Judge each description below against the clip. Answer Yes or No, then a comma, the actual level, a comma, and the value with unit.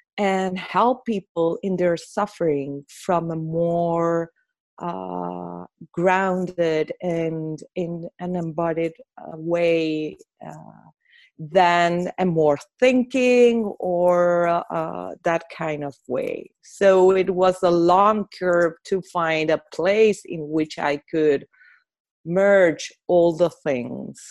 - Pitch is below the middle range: No, medium, 175 Hz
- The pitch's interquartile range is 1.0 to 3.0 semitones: Yes, average, 2.7 semitones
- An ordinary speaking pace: No, slow, 110 wpm